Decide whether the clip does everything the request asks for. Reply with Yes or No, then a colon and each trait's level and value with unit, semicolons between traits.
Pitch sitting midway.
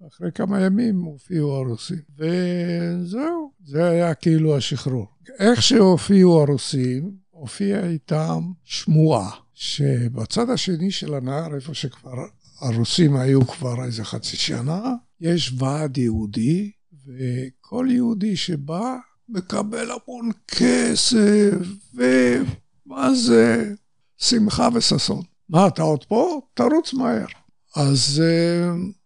Yes: medium, 170 Hz